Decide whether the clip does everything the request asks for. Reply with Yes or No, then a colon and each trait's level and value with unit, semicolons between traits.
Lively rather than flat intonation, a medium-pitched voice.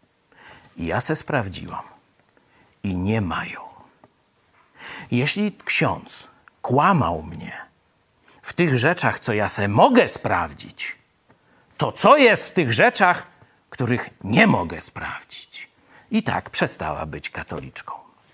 No: wide, 7.8 semitones; low, 120 Hz